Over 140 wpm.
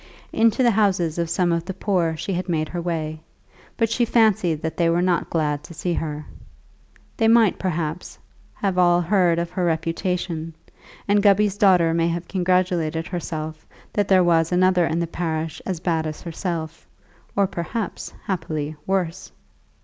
Yes: average, 165 wpm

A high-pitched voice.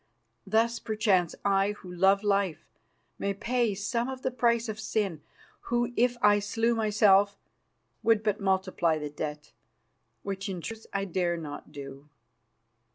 Yes: high, 200 Hz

